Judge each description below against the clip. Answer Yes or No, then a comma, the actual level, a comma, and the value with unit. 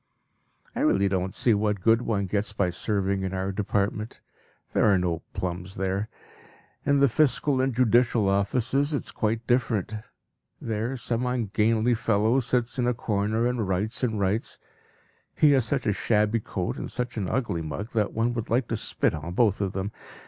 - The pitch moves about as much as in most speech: Yes, average, 3.6 semitones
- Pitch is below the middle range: Yes, low, 110 Hz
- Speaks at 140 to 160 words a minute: No, average, 180 wpm